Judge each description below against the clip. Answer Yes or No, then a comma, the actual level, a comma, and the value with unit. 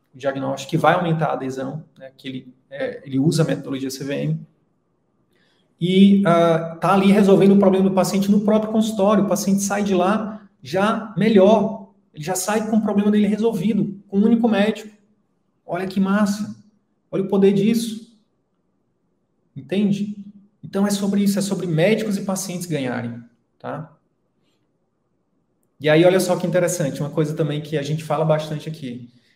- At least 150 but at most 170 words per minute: Yes, average, 165 wpm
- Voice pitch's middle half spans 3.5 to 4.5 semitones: No, average, 4.9 semitones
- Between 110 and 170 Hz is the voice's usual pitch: No, high, 190 Hz